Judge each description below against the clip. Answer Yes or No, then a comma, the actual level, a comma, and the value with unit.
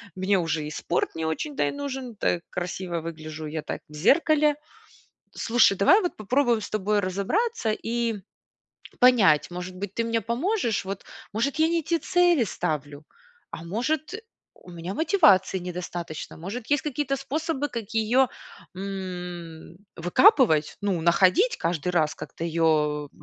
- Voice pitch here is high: Yes, high, 200 Hz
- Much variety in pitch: Yes, wide, 7.7 semitones